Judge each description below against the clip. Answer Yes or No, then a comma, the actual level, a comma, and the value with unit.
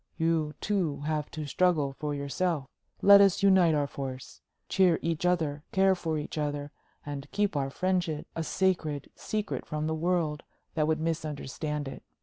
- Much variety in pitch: No, average, 3.5 semitones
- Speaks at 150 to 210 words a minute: Yes, average, 160 wpm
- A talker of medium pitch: Yes, medium, 155 Hz